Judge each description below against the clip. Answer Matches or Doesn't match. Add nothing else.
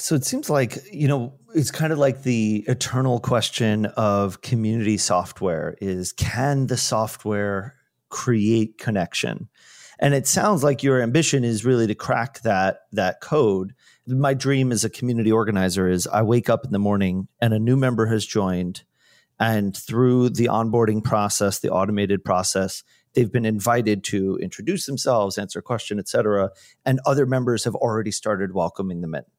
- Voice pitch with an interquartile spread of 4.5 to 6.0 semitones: Doesn't match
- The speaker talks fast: Doesn't match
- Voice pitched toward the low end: Matches